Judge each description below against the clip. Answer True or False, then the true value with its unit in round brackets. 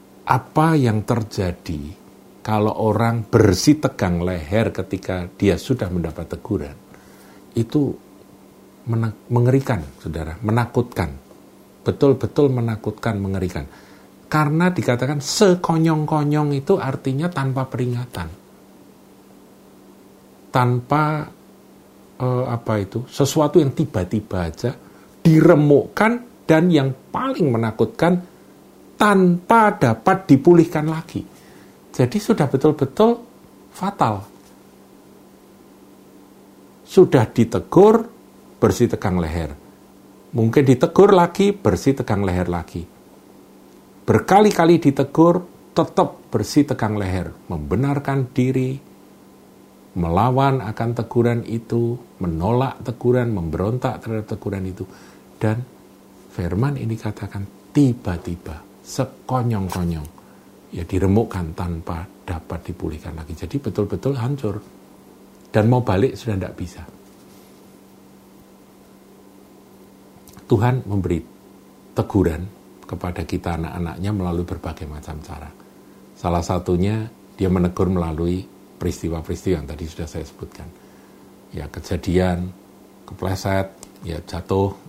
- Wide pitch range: True (6.7 semitones)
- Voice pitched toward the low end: True (110 Hz)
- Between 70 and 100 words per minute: True (90 wpm)